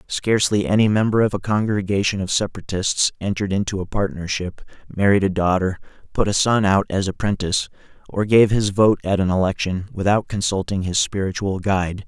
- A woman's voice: No, male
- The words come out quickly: No, average, 165 wpm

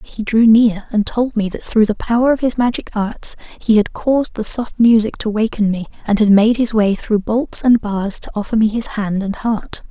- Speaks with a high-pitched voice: Yes, high, 220 Hz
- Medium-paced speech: No, fast, 235 wpm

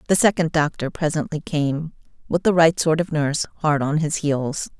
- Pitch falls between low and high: Yes, medium, 155 Hz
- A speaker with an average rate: Yes, average, 190 wpm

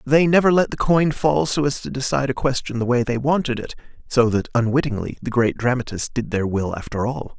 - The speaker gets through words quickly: Yes, fast, 230 wpm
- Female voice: No, male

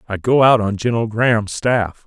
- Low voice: Yes, low, 110 Hz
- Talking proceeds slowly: No, fast, 205 wpm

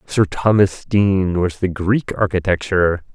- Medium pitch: No, very low, 95 Hz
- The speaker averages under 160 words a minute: Yes, slow, 135 wpm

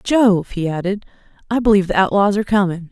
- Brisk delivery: No, average, 185 wpm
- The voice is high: Yes, high, 195 Hz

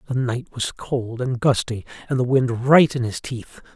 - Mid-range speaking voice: No, low, 125 Hz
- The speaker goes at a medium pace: No, fast, 210 wpm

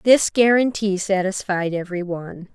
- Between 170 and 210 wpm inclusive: No, slow, 120 wpm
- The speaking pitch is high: Yes, high, 195 Hz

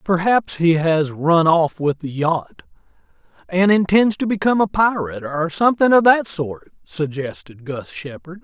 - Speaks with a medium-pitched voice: Yes, medium, 170 Hz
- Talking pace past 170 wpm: No, average, 155 wpm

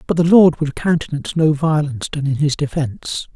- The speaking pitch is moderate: Yes, medium, 150 Hz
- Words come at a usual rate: Yes, average, 195 wpm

